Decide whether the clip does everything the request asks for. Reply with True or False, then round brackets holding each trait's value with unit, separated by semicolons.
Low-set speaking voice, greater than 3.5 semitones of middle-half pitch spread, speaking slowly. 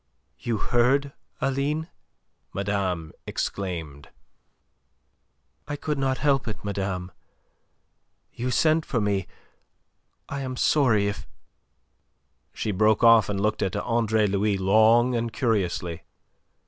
True (110 Hz; 4.6 semitones; 110 wpm)